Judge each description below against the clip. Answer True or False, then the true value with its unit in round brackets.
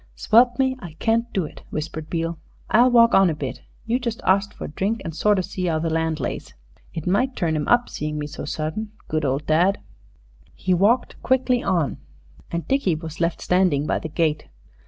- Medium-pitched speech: True (175 Hz)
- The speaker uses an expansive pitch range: True (6.1 semitones)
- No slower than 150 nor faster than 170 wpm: False (205 wpm)